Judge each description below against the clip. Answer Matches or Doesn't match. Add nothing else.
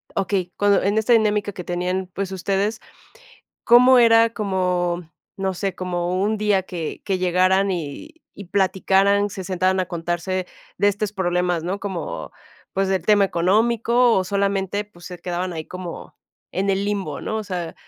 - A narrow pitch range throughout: Matches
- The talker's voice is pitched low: Doesn't match